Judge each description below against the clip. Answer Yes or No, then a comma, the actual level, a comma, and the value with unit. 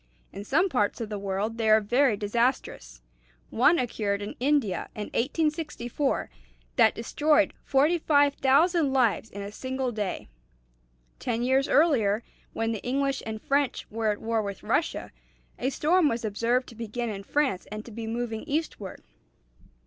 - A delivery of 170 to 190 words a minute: No, average, 150 wpm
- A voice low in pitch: No, high, 235 Hz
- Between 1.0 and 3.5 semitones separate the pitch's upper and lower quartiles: No, average, 4.7 semitones